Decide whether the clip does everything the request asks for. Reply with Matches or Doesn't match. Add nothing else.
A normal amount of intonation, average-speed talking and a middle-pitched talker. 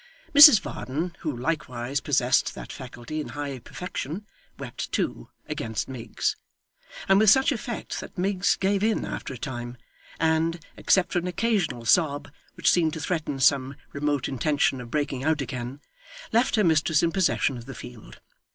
Doesn't match